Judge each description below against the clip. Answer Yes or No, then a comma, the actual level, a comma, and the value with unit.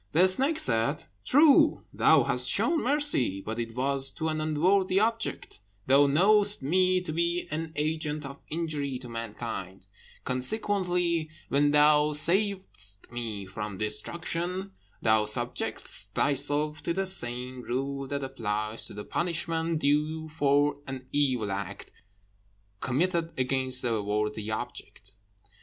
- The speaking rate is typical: No, slow, 130 wpm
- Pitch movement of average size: No, wide, 6.2 semitones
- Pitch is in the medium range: Yes, medium, 145 Hz